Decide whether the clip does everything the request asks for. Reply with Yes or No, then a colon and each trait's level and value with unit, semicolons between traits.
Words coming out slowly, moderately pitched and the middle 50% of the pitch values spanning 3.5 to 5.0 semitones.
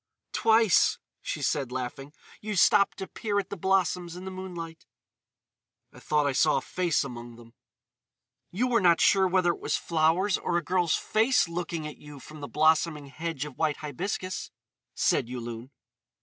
No: average, 170 wpm; medium, 165 Hz; average, 4.2 semitones